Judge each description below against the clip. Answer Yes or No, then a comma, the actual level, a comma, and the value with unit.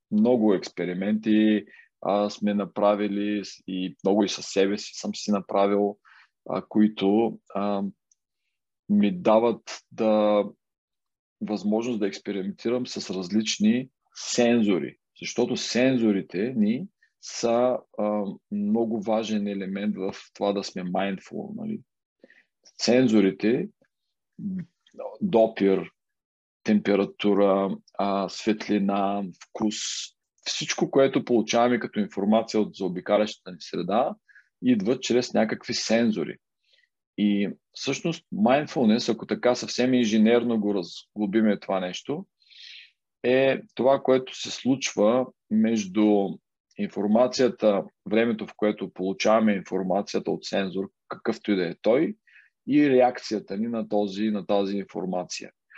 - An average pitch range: Yes, average, 3.4 semitones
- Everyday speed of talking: No, slow, 105 wpm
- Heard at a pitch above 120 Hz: No, low, 105 Hz